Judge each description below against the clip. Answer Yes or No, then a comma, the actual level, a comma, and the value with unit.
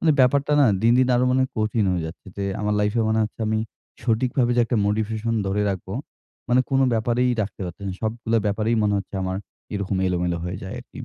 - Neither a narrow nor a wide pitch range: Yes, average, 3.4 semitones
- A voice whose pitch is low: Yes, low, 110 Hz